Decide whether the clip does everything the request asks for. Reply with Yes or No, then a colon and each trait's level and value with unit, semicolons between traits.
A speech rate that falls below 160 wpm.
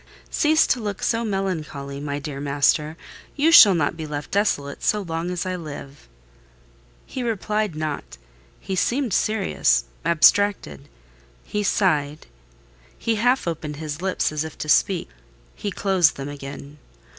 Yes: average, 140 wpm